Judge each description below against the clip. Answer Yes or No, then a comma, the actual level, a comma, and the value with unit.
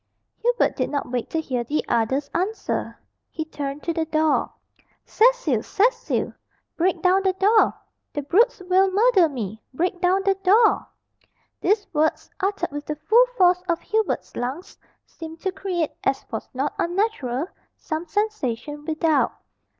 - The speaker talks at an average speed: Yes, average, 150 wpm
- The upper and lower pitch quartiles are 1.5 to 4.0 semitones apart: No, average, 5.1 semitones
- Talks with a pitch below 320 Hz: No, very high, 340 Hz